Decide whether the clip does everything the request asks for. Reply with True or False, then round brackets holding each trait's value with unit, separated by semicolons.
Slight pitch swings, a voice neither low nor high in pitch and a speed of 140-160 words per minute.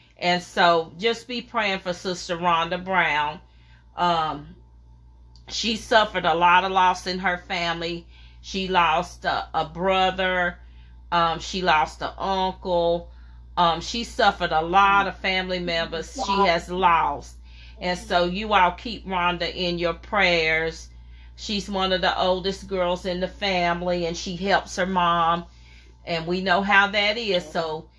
True (2.3 semitones; 175 Hz; 150 wpm)